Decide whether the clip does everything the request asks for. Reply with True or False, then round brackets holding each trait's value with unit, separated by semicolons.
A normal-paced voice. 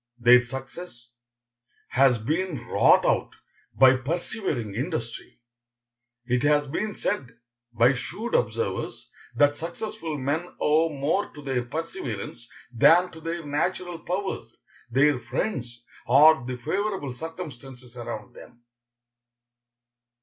False (110 wpm)